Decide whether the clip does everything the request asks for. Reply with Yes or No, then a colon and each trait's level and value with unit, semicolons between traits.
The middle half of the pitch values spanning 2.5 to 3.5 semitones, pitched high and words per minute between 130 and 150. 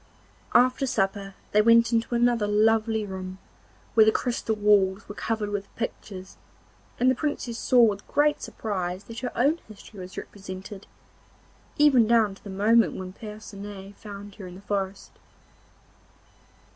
Yes: average, 2.8 semitones; high, 210 Hz; average, 145 wpm